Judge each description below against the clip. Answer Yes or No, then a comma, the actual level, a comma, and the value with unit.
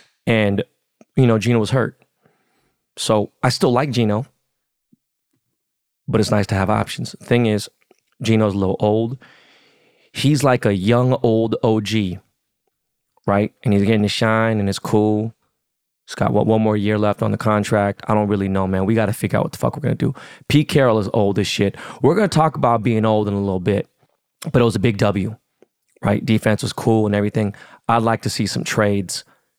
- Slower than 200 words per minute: No, fast, 205 wpm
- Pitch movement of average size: No, narrow, 2.0 semitones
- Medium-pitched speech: No, low, 110 Hz